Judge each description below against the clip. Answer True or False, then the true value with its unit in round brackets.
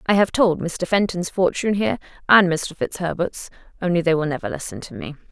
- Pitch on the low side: False (185 Hz)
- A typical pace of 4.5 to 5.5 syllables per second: False (5.8 syllables/s)